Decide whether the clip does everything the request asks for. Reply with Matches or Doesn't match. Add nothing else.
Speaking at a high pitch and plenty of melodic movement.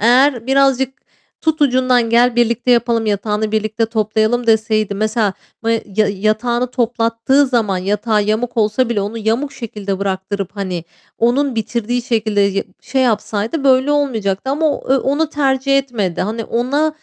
Doesn't match